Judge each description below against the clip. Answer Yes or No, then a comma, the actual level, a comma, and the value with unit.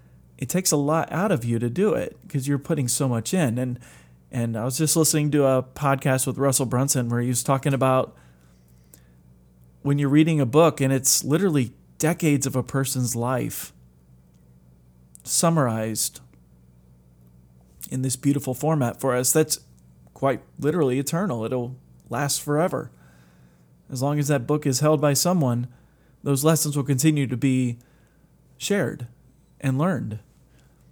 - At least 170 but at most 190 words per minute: No, average, 150 wpm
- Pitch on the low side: Yes, low, 130 Hz